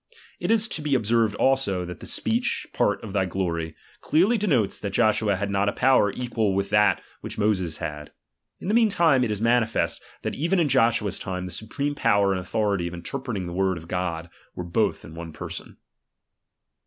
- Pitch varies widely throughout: Yes, wide, 6.3 semitones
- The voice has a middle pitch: No, low, 105 Hz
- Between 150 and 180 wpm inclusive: No, average, 190 wpm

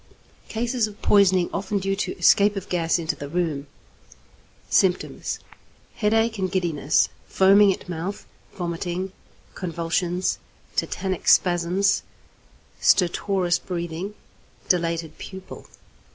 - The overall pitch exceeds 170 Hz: Yes, medium, 185 Hz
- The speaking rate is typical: No, slow, 100 wpm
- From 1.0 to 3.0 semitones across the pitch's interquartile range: Yes, narrow, 2.6 semitones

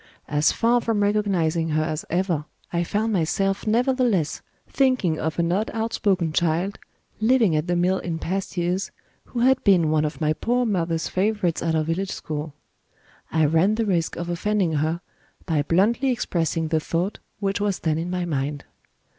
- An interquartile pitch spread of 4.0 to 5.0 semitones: Yes, average, 4.3 semitones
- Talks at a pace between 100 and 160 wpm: No, average, 170 wpm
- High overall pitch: No, medium, 175 Hz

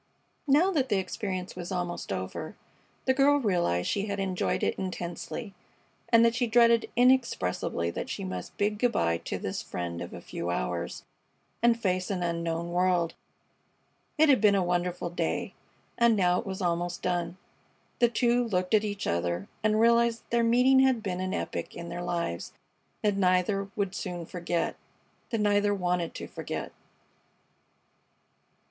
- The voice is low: No, medium, 185 Hz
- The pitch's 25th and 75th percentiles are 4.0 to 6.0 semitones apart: Yes, average, 4.8 semitones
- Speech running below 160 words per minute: No, average, 165 wpm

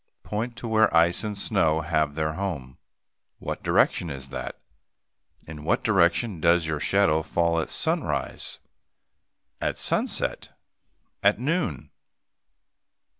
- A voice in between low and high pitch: No, very low, 85 Hz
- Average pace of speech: No, slow, 120 wpm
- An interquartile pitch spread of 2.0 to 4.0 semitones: No, average, 4.7 semitones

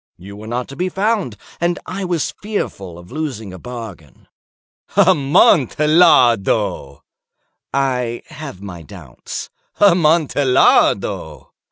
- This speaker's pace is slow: Yes, slow, 100 wpm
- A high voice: No, low, 130 Hz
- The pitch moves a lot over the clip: Yes, wide, 9.0 semitones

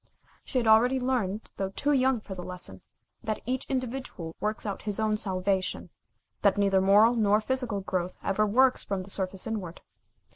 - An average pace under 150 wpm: No, average, 175 wpm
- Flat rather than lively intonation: No, average, 4.2 semitones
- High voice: Yes, high, 210 Hz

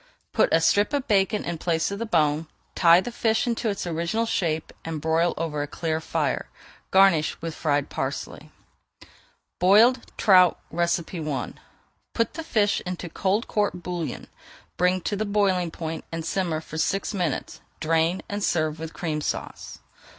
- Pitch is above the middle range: No, medium, 175 Hz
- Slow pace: No, average, 160 wpm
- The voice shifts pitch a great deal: No, average, 3.8 semitones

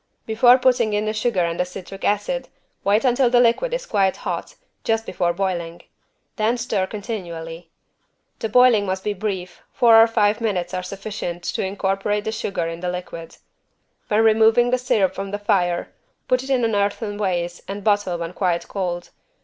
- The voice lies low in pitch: No, high, 205 Hz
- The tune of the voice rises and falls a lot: No, average, 3.7 semitones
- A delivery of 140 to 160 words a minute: No, average, 180 wpm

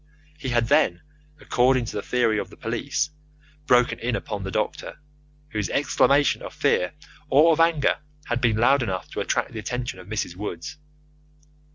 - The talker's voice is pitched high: No, low, 120 Hz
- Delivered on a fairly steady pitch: No, average, 4.0 semitones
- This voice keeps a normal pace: Yes, average, 170 wpm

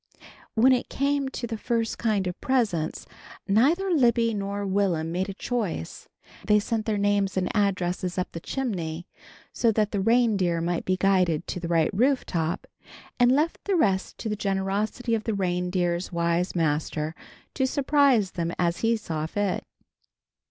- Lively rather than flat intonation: No, average, 4.7 semitones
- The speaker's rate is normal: Yes, average, 165 wpm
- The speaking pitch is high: Yes, high, 200 Hz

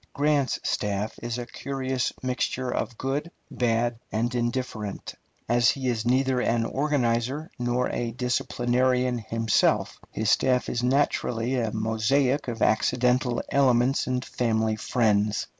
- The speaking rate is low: Yes, slow, 125 wpm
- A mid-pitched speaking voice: No, low, 120 Hz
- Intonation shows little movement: Yes, narrow, 2.2 semitones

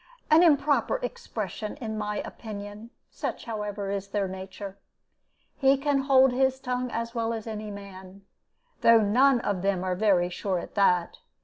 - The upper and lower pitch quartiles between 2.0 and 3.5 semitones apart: No, average, 4.2 semitones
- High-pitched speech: Yes, high, 215 Hz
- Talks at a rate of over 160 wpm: No, average, 155 wpm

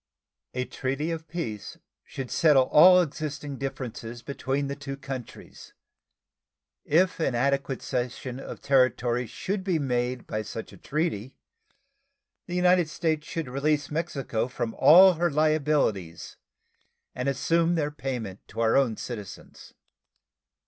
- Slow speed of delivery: Yes, slow, 130 wpm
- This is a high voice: No, medium, 140 Hz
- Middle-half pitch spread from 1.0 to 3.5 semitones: No, average, 4.0 semitones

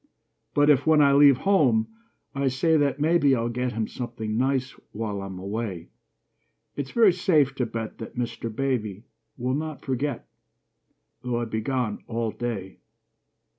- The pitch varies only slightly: No, average, 4.1 semitones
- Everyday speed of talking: Yes, average, 155 wpm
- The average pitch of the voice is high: No, low, 125 Hz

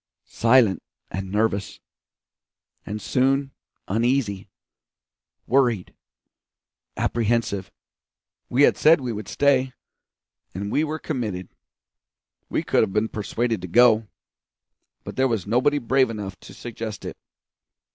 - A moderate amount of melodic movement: Yes, average, 4.2 semitones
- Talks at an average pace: No, slow, 115 wpm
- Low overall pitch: Yes, low, 115 Hz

